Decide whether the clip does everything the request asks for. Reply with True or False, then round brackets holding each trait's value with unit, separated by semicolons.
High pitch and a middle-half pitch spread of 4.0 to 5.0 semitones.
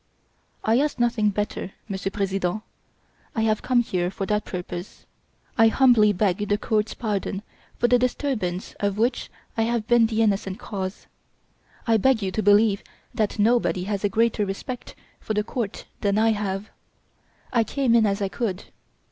False (210 Hz; 2.7 semitones)